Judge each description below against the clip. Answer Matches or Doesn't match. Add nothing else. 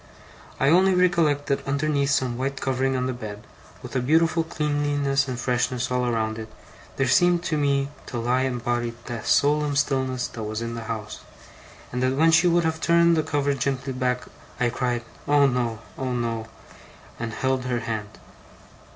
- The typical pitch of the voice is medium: Doesn't match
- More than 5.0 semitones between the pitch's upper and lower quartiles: Doesn't match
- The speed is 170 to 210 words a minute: Matches